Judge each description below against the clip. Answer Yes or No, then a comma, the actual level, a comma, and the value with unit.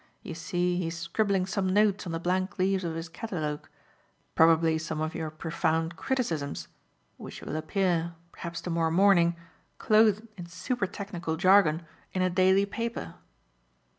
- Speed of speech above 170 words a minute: No, average, 155 wpm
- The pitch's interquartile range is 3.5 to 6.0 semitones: No, average, 3.1 semitones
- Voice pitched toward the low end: No, medium, 175 Hz